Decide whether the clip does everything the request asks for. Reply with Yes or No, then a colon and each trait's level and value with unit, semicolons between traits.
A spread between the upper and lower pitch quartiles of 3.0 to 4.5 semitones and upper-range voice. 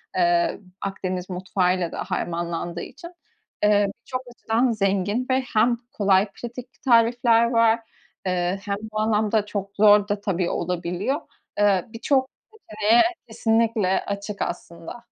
Yes: average, 3.7 semitones; high, 210 Hz